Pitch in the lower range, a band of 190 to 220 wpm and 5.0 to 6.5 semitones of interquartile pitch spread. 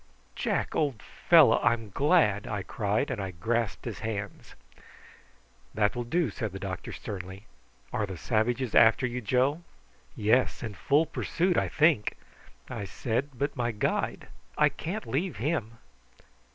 No: low, 115 Hz; average, 145 wpm; average, 5.3 semitones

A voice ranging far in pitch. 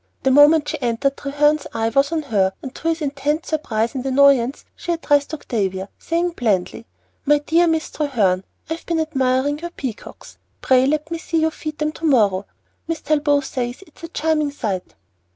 No: average, 4.1 semitones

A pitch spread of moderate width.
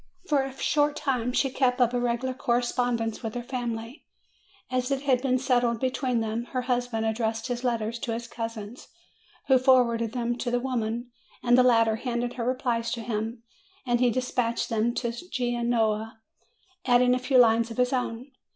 No: narrow, 1.6 semitones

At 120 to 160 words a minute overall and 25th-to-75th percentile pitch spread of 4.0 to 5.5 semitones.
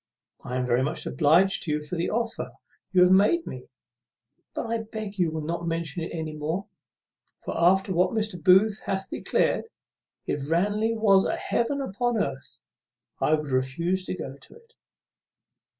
No: average, 170 wpm; average, 5.2 semitones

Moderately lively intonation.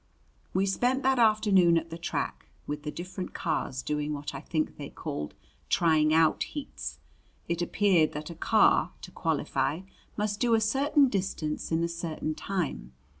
Yes: average, 5.0 semitones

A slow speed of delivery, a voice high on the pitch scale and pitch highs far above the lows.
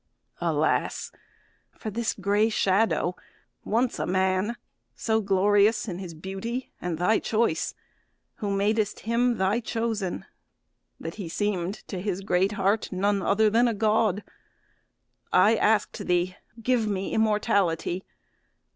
No: slow, 125 wpm; high, 205 Hz; average, 2.7 semitones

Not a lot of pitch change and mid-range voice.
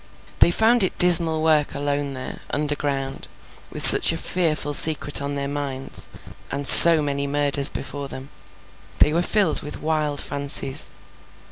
Yes: narrow, 2.0 semitones; medium, 145 Hz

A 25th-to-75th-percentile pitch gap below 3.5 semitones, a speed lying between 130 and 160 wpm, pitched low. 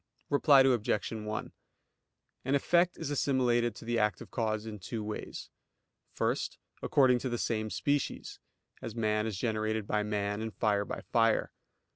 Yes: average, 3.0 semitones; average, 150 wpm; low, 110 Hz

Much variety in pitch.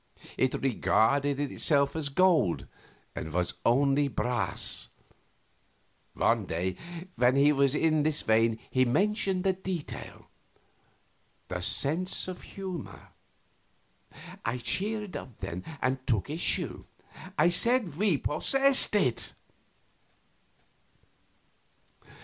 Yes: wide, 6.7 semitones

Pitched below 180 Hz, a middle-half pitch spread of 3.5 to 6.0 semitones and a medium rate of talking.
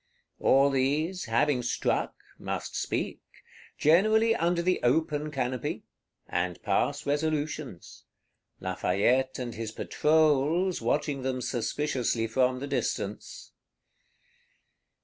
No: medium, 140 Hz; average, 4.1 semitones; slow, 90 wpm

